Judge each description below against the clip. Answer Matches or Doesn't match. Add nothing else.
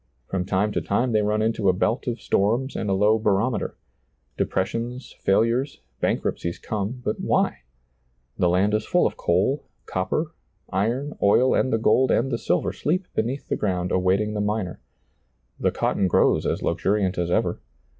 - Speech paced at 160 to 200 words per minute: Matches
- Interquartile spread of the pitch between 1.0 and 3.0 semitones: Doesn't match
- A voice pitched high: Doesn't match